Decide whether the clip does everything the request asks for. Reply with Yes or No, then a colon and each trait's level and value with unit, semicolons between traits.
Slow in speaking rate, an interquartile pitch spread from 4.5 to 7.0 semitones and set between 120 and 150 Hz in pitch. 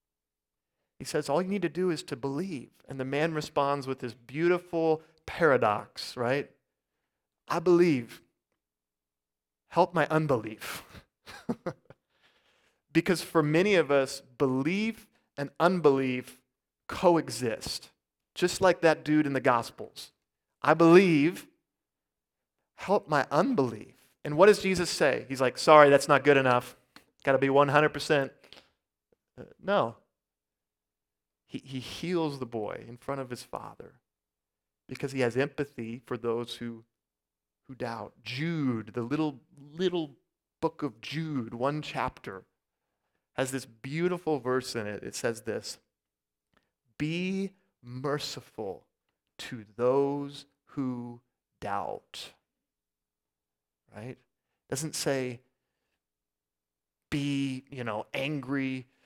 Yes: slow, 115 wpm; average, 4.8 semitones; low, 135 Hz